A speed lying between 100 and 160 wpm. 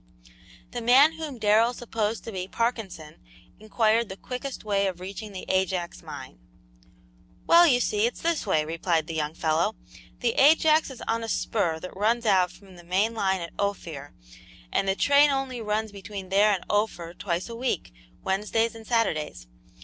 No: average, 170 wpm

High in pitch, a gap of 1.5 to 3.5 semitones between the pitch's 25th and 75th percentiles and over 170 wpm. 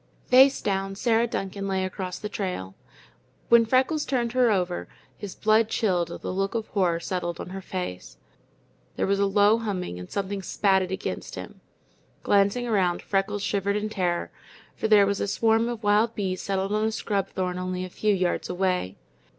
Yes: high, 195 Hz; average, 2.7 semitones; average, 185 wpm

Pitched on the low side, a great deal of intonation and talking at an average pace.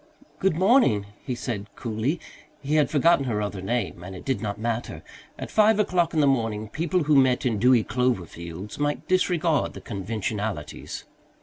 Yes: low, 125 Hz; wide, 6.7 semitones; average, 175 wpm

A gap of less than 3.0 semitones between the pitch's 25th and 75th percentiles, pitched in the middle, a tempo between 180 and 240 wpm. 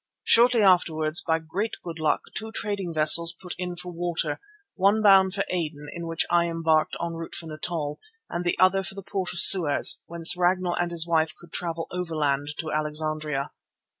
Yes: narrow, 2.5 semitones; medium, 170 Hz; average, 185 wpm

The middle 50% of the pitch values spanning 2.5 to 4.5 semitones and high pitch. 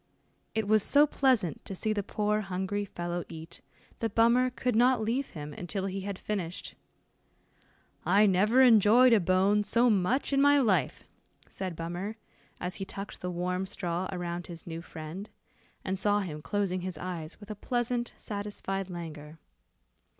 Yes: average, 3.5 semitones; high, 195 Hz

